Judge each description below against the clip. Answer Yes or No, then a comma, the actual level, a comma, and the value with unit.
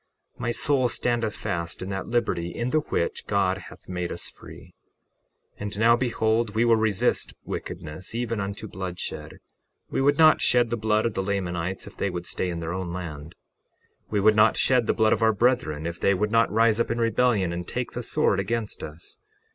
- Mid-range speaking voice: No, low, 105 Hz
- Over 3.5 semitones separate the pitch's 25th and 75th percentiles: Yes, average, 4.5 semitones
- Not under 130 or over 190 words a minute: No, fast, 205 wpm